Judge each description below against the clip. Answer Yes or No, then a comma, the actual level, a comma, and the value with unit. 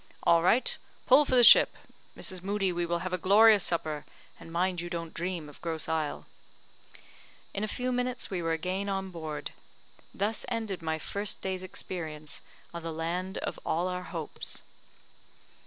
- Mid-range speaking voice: Yes, medium, 180 Hz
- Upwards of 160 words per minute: Yes, average, 170 wpm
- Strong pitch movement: No, average, 3.2 semitones